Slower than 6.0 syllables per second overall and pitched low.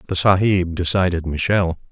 Yes: 5.6 syllables/s; very low, 90 Hz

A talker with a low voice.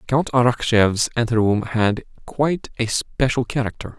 Yes: low, 120 Hz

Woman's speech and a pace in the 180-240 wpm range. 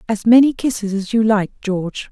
Yes: female; average, 200 wpm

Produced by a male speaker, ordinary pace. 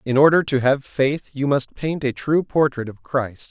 No: male; fast, 220 wpm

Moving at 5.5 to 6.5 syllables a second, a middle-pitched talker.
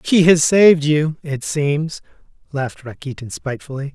No: 4.9 syllables/s; medium, 150 Hz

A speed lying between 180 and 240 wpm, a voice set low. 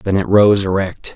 Yes: fast, 205 wpm; very low, 95 Hz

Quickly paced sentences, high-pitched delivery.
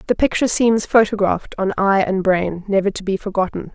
No: average, 190 wpm; high, 200 Hz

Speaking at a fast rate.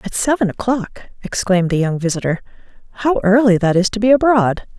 No: average, 175 wpm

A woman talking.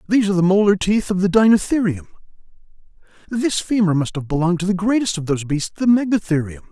No: male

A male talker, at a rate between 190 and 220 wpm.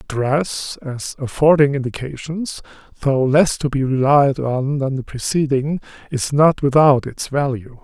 No: male; average, 140 wpm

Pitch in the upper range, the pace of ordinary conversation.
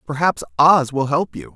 No: medium, 140 Hz; average, 190 wpm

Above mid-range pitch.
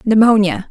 Yes: high, 200 Hz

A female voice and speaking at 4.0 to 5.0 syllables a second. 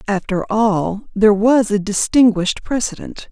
Yes: female; 4.5 syllables/s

